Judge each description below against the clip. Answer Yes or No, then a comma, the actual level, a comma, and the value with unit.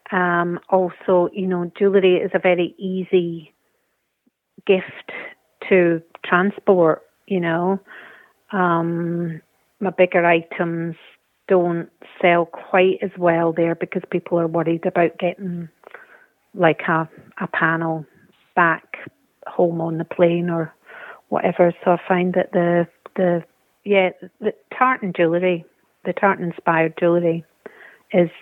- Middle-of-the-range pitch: Yes, medium, 175 Hz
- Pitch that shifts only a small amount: Yes, narrow, 1.8 semitones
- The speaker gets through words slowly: Yes, slow, 120 wpm